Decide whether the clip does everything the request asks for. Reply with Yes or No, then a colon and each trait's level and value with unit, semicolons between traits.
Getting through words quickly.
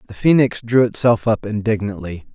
No: average, 155 wpm